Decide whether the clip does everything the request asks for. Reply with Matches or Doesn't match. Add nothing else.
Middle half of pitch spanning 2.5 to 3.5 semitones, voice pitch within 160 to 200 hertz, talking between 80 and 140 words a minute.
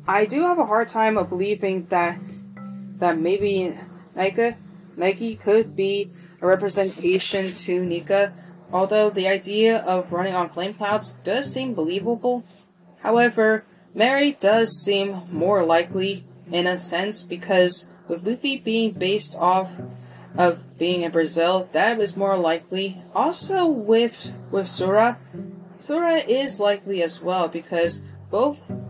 Matches